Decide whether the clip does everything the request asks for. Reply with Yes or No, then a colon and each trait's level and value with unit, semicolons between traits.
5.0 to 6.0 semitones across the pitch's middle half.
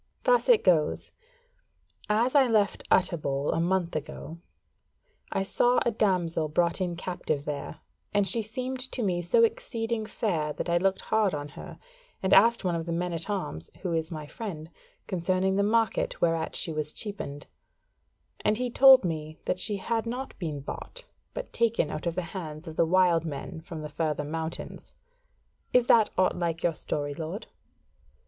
Yes: average, 5.3 semitones